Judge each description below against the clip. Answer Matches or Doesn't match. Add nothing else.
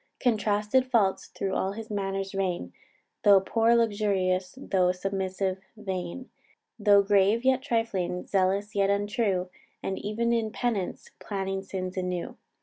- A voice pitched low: Doesn't match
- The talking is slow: Matches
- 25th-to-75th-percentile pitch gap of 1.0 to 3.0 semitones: Matches